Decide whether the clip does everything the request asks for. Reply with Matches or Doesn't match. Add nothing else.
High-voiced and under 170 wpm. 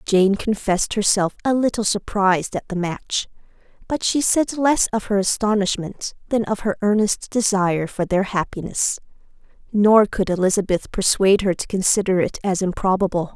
Matches